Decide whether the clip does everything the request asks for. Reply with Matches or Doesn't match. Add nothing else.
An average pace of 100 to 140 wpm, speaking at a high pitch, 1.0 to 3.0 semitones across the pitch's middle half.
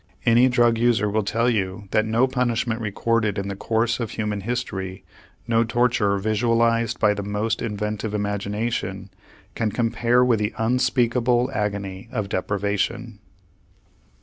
Doesn't match